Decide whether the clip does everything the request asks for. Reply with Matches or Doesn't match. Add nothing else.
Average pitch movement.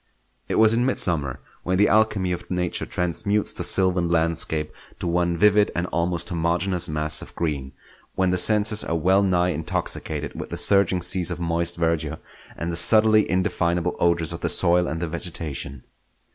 Doesn't match